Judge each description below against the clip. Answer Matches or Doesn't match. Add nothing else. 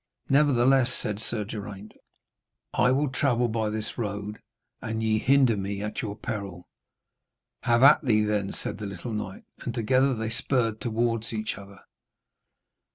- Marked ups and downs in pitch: Doesn't match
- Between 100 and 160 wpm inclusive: Matches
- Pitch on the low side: Matches